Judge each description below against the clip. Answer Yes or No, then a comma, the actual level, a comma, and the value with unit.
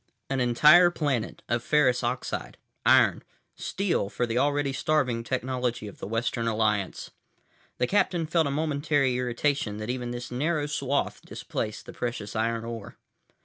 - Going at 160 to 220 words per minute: No, average, 140 wpm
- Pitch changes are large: No, average, 3.9 semitones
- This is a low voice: Yes, low, 125 Hz